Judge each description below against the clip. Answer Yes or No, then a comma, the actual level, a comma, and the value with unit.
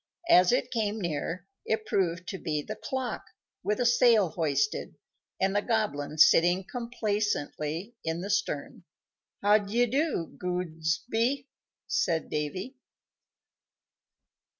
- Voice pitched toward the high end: Yes, high, 200 Hz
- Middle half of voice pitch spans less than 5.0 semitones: No, wide, 5.6 semitones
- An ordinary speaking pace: No, slow, 115 wpm